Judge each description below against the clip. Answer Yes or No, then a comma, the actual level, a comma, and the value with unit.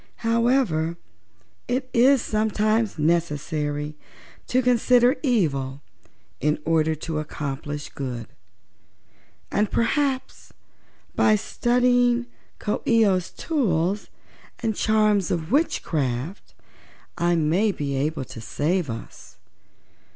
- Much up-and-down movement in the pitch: Yes, wide, 7.6 semitones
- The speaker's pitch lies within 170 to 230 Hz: Yes, medium, 185 Hz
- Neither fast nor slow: No, slow, 95 wpm